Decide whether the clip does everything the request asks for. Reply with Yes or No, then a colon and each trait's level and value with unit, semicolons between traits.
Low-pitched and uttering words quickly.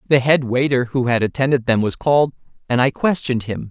Yes: low, 130 Hz; fast, 210 wpm